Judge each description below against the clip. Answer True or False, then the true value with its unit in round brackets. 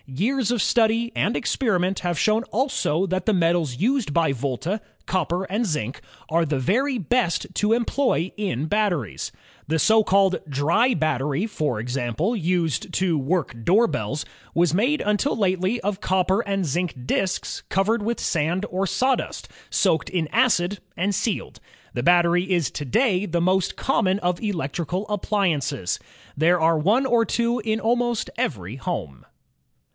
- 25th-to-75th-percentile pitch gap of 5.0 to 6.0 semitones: True (5.3 semitones)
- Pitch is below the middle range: False (185 Hz)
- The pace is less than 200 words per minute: True (155 wpm)